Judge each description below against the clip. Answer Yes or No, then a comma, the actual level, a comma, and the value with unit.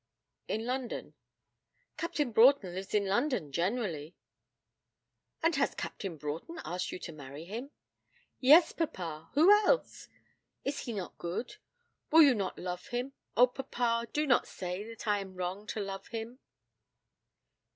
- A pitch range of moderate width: No, wide, 6.7 semitones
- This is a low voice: No, high, 220 Hz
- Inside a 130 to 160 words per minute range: Yes, average, 140 wpm